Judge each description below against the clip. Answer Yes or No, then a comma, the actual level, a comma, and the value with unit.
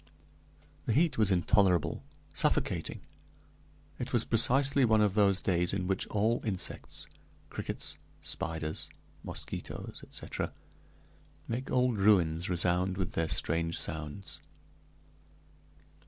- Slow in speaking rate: Yes, slow, 105 wpm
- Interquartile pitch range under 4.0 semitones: No, average, 4.3 semitones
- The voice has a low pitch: Yes, very low, 95 Hz